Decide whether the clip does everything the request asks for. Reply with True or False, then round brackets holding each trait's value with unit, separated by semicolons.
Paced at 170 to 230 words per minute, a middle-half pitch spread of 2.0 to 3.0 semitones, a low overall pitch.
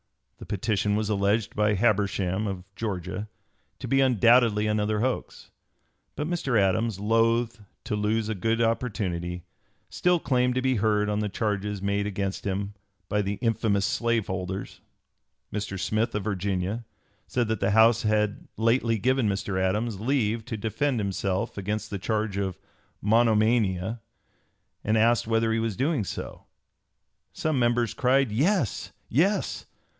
False (145 wpm; 2.6 semitones; 110 Hz)